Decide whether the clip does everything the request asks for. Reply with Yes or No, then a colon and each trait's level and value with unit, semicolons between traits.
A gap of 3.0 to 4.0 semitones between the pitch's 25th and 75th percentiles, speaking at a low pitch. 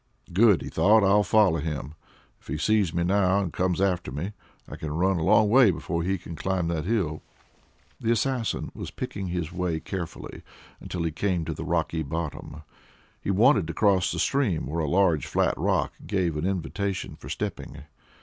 Yes: average, 3.5 semitones; very low, 90 Hz